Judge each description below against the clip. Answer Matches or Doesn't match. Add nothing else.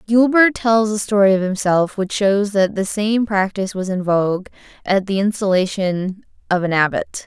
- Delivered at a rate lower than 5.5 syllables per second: Matches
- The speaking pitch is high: Matches